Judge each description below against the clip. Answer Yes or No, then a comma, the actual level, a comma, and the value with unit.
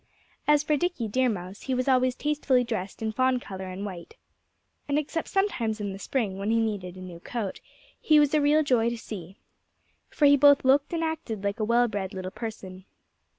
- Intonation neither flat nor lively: No, wide, 6.3 semitones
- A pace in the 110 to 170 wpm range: No, fast, 205 wpm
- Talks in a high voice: Yes, high, 235 Hz